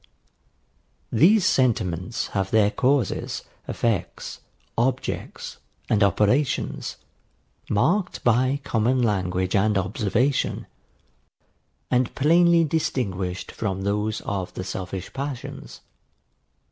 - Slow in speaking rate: Yes, slow, 85 wpm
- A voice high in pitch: No, low, 110 Hz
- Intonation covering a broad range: Yes, wide, 5.7 semitones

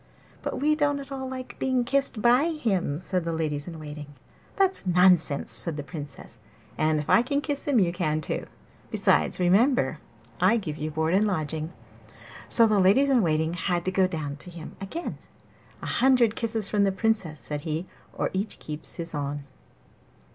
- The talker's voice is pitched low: No, medium, 185 Hz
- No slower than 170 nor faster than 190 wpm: Yes, average, 185 wpm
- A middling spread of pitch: No, wide, 7.5 semitones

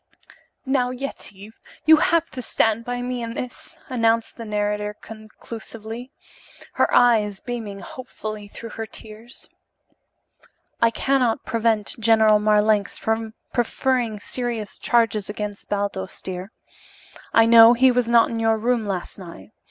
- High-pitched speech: Yes, high, 225 Hz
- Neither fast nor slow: No, slow, 130 wpm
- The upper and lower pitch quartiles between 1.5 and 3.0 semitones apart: Yes, narrow, 2.4 semitones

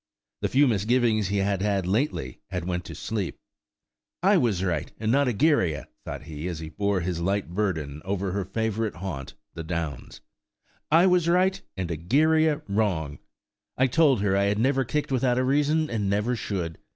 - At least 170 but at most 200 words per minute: Yes, average, 175 wpm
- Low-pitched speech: Yes, low, 100 Hz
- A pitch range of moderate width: No, wide, 6.4 semitones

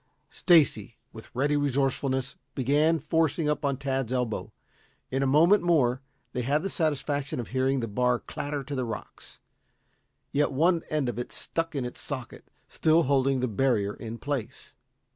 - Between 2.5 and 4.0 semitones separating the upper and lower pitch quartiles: Yes, average, 3.1 semitones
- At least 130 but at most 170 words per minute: Yes, average, 165 wpm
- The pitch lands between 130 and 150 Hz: Yes, low, 135 Hz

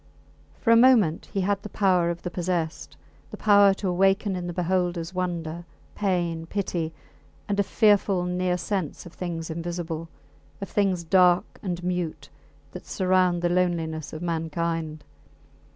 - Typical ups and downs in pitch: No, narrow, 2.3 semitones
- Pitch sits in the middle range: Yes, medium, 180 Hz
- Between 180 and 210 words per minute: No, average, 150 wpm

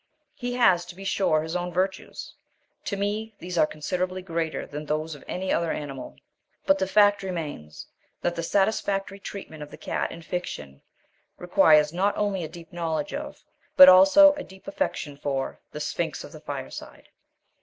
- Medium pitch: Yes, medium, 180 Hz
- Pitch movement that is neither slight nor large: Yes, average, 4.0 semitones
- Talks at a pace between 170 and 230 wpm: Yes, average, 175 wpm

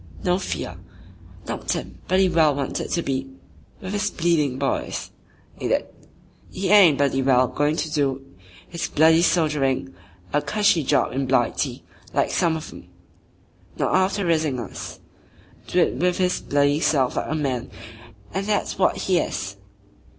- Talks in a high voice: No, medium, 155 Hz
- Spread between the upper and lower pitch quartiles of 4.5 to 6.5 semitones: Yes, average, 4.9 semitones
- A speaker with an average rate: Yes, average, 160 wpm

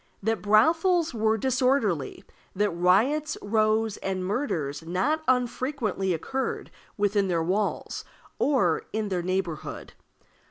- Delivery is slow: Yes, slow, 110 wpm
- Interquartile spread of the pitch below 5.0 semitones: No, wide, 5.6 semitones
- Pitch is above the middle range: Yes, high, 210 Hz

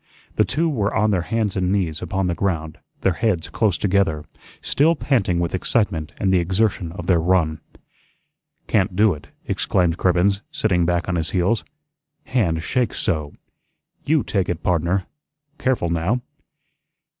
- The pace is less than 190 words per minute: Yes, average, 155 wpm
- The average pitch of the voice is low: Yes, very low, 90 Hz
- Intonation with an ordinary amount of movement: Yes, average, 3.6 semitones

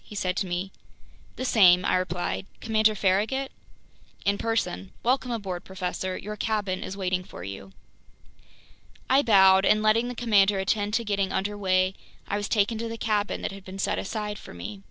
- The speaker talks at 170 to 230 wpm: Yes, average, 180 wpm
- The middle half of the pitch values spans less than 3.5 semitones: Yes, average, 2.7 semitones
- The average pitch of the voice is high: Yes, high, 200 Hz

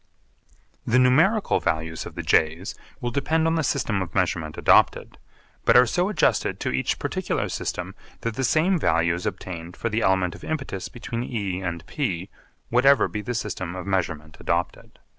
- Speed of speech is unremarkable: Yes, average, 175 wpm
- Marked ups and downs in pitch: Yes, wide, 7.1 semitones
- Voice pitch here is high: No, low, 100 Hz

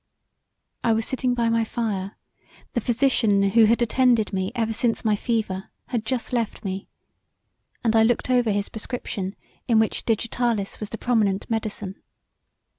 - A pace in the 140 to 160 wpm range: Yes, average, 155 wpm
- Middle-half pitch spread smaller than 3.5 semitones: Yes, narrow, 2.6 semitones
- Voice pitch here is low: No, high, 225 Hz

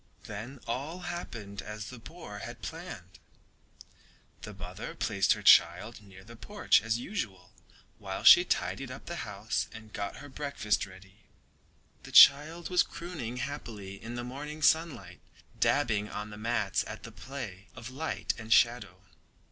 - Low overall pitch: Yes, low, 115 Hz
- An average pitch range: No, wide, 5.7 semitones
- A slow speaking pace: No, average, 150 wpm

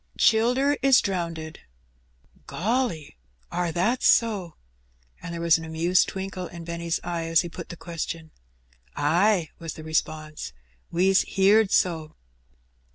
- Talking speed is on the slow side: Yes, slow, 130 wpm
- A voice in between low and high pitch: Yes, medium, 170 Hz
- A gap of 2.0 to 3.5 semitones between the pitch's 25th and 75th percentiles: Yes, average, 3.0 semitones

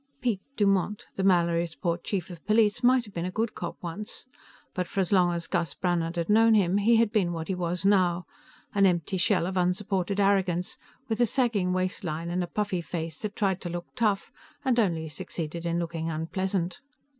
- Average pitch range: Yes, average, 3.1 semitones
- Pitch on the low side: No, medium, 185 Hz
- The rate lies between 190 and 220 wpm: Yes, average, 195 wpm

